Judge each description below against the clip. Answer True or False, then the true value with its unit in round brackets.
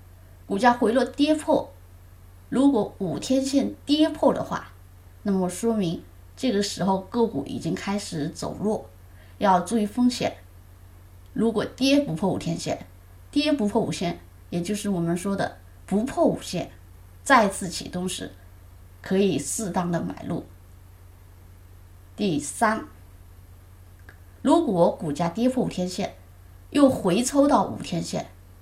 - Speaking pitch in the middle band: True (165 Hz)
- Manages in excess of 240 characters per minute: False (190 characters per minute)